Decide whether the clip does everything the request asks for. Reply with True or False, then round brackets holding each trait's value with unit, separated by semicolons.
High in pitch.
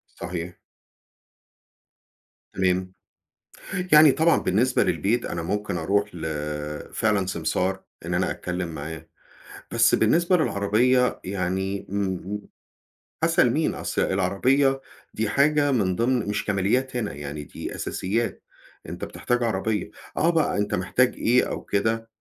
False (105 Hz)